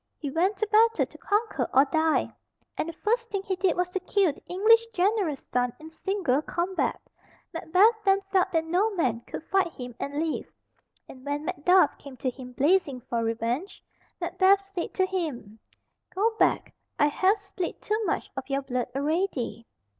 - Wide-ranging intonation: Yes, wide, 5.9 semitones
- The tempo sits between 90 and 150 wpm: No, average, 175 wpm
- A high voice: Yes, very high, 345 Hz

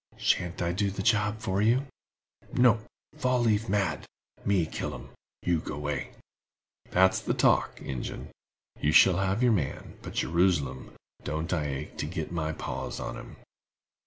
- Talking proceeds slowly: No, average, 150 wpm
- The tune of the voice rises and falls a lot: No, average, 5.0 semitones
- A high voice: No, very low, 95 Hz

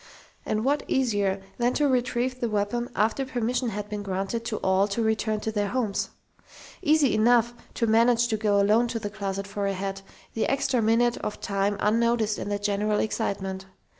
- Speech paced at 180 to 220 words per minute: Yes, average, 185 wpm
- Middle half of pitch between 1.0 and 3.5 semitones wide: Yes, average, 2.8 semitones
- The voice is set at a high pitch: Yes, high, 220 Hz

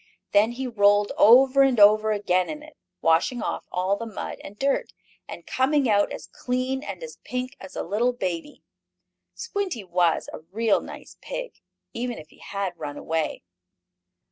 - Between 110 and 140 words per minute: No, average, 170 wpm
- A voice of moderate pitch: No, high, 220 Hz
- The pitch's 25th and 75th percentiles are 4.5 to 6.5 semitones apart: Yes, wide, 5.4 semitones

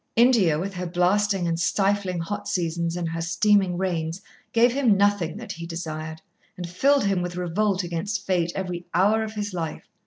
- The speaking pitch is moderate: Yes, medium, 180 Hz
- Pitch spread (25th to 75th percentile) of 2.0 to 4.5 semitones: Yes, average, 3.2 semitones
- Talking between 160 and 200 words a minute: Yes, average, 180 wpm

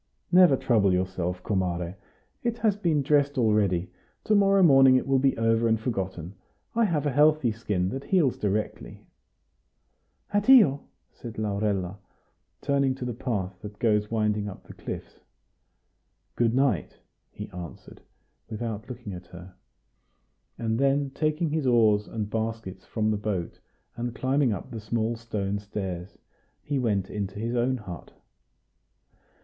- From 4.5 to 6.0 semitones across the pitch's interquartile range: Yes, average, 5.1 semitones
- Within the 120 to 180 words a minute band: Yes, average, 145 wpm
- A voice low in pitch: Yes, low, 115 Hz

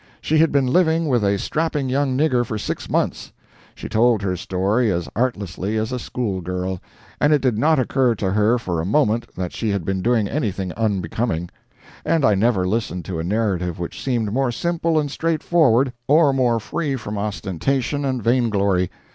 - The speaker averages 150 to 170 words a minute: No, average, 190 wpm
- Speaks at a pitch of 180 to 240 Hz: No, low, 115 Hz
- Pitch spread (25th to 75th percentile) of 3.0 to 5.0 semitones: No, wide, 5.6 semitones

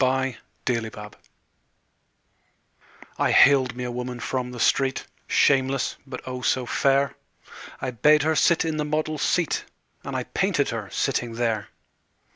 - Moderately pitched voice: No, low, 130 Hz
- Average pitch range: No, narrow, 2.3 semitones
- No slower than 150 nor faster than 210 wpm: No, average, 140 wpm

